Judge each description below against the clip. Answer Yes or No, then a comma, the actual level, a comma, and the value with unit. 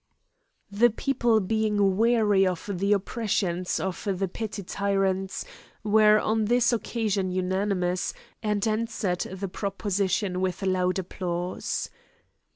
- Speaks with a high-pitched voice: Yes, high, 200 Hz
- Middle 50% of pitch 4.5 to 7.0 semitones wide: No, narrow, 2.6 semitones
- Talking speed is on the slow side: Yes, slow, 110 wpm